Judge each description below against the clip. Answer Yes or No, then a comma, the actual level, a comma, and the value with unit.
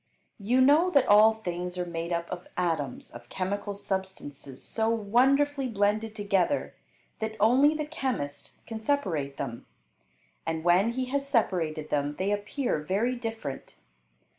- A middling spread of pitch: No, wide, 6.1 semitones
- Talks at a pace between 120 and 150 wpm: Yes, average, 140 wpm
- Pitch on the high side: Yes, high, 205 Hz